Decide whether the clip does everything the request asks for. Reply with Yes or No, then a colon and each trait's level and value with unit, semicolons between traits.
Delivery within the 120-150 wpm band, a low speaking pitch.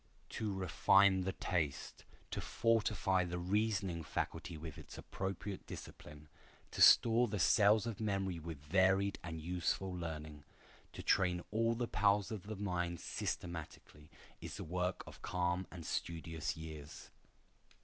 Yes: average, 140 wpm; very low, 90 Hz